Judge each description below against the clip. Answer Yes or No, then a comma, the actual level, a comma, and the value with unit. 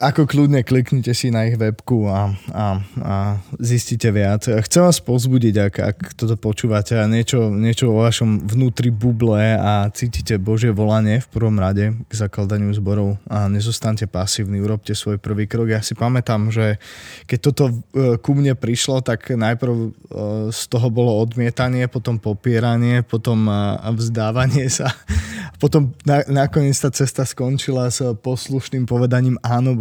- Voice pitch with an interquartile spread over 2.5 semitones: Yes, average, 2.9 semitones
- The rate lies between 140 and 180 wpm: Yes, average, 145 wpm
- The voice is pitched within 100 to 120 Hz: Yes, low, 115 Hz